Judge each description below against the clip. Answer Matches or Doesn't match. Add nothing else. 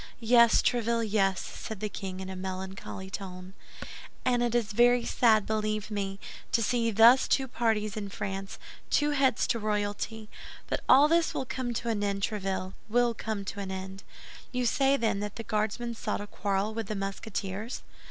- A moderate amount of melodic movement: Matches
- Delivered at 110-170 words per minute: Doesn't match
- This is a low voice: Doesn't match